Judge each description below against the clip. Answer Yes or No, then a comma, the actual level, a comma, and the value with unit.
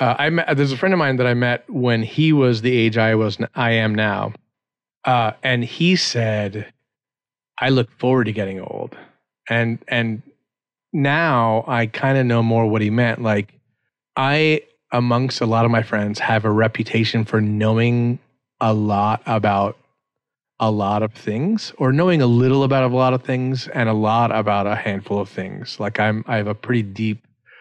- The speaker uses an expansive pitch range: No, average, 2.9 semitones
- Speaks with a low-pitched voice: Yes, low, 115 Hz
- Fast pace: No, average, 185 wpm